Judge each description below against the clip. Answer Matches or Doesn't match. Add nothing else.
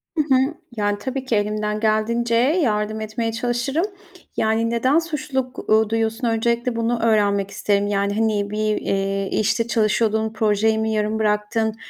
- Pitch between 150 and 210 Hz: Doesn't match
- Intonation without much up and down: Matches